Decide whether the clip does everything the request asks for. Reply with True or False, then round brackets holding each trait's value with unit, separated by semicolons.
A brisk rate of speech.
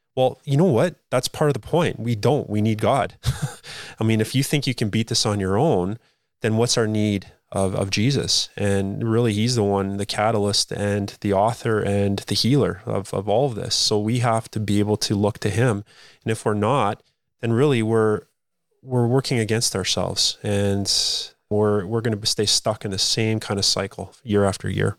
True (210 wpm)